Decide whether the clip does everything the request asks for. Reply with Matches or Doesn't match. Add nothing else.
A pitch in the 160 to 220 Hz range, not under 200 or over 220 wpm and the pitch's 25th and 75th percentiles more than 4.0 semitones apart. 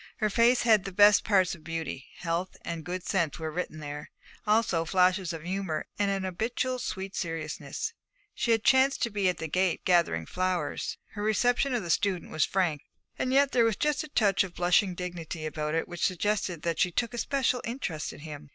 Matches